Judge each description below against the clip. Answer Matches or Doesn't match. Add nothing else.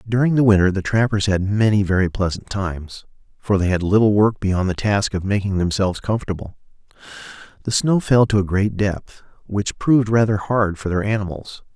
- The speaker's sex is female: Doesn't match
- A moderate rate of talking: Matches